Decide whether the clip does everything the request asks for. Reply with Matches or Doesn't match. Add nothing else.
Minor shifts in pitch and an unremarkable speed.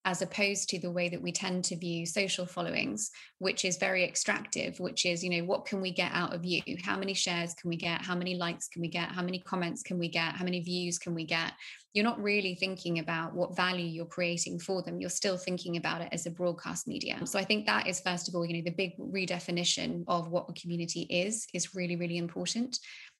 Doesn't match